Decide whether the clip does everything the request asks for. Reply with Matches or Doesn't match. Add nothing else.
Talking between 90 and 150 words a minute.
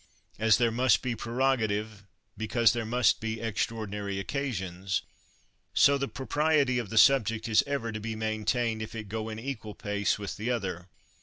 Doesn't match